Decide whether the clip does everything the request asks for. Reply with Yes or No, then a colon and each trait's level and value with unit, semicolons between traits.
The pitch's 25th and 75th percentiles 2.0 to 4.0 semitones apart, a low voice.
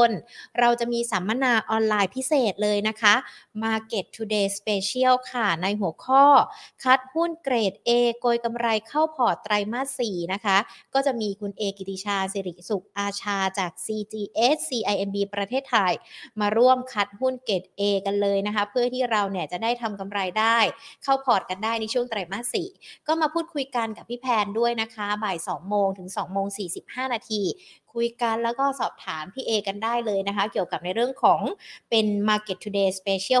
No: average, 3.5 semitones; high, 220 Hz